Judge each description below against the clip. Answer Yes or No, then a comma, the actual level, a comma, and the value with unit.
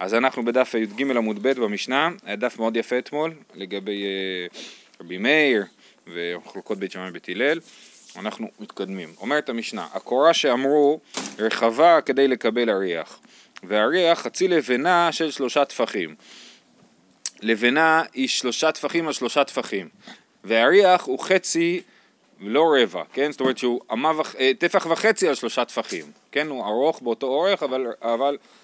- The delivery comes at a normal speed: Yes, average, 140 wpm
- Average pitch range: No, wide, 5.9 semitones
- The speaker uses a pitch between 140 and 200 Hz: No, low, 130 Hz